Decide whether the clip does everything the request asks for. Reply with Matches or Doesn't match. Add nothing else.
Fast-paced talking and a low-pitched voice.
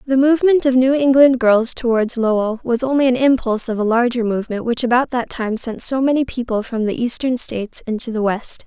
Doesn't match